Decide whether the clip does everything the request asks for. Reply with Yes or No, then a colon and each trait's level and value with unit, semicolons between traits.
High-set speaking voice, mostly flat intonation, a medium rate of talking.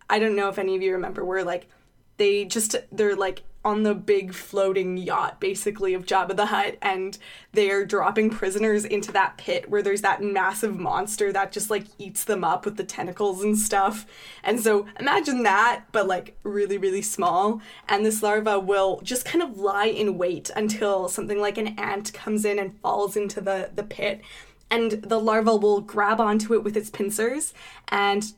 Yes: high, 205 Hz; narrow, 1.6 semitones; average, 190 wpm